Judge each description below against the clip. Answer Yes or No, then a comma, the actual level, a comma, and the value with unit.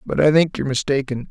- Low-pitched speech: Yes, low, 130 Hz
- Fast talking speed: Yes, fast, 230 wpm